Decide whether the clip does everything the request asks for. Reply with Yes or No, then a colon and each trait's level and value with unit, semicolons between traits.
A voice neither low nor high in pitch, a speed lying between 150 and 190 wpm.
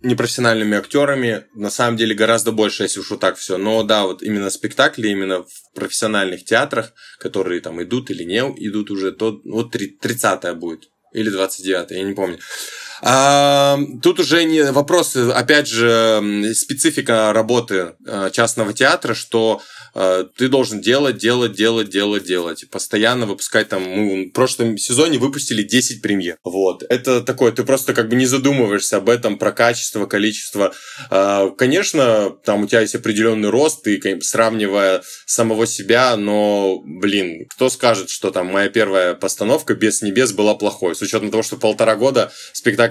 No: low, 110 Hz; fast, 160 wpm